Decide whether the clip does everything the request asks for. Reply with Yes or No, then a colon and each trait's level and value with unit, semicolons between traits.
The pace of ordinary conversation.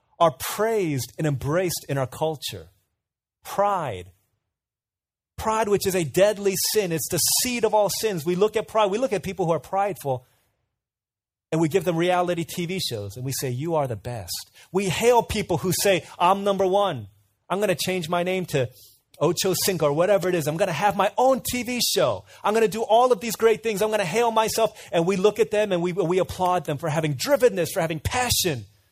No: fast, 215 wpm